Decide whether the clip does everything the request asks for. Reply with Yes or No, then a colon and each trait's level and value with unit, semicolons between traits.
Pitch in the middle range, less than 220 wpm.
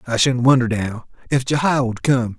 No: low, 125 Hz; average, 200 wpm